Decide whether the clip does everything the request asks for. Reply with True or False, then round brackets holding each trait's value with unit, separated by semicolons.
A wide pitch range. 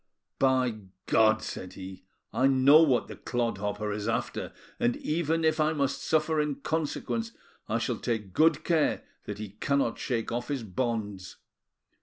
True (5.8 semitones)